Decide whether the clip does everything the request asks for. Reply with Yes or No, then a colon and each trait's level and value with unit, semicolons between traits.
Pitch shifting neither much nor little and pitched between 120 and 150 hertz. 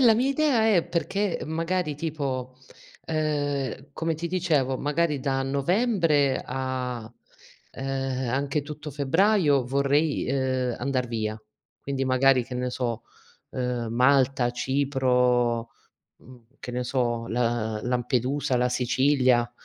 Yes: average, 3.1 semitones; low, 135 Hz